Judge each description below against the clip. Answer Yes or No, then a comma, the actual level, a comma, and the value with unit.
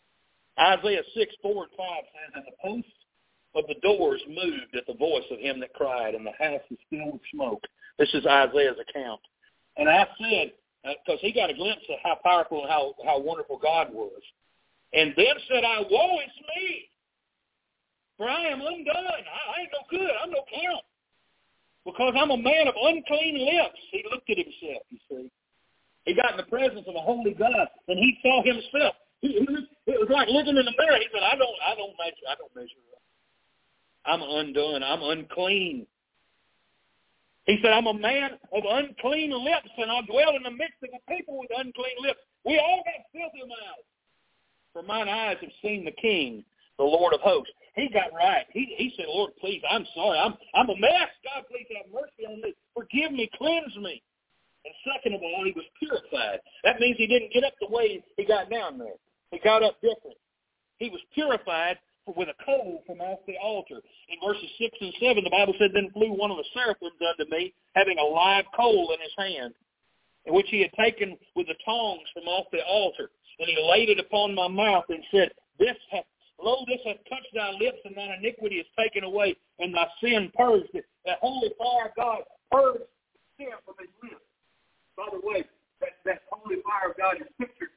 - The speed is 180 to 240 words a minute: Yes, average, 200 wpm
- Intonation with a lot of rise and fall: Yes, wide, 8.4 semitones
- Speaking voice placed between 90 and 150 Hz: No, high, 245 Hz